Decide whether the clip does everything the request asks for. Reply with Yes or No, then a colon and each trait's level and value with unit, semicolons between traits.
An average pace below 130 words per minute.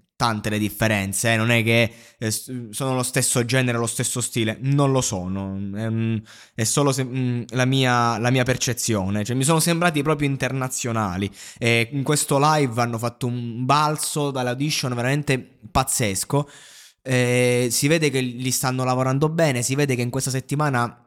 No: average, 155 wpm